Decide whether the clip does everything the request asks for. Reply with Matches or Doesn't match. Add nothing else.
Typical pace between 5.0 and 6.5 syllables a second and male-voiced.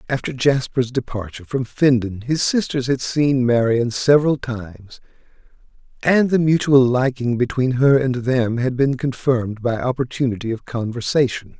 Doesn't match